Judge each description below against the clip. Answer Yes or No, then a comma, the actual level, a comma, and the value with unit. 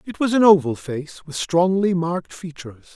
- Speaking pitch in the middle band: Yes, medium, 170 Hz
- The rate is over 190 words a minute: No, average, 185 wpm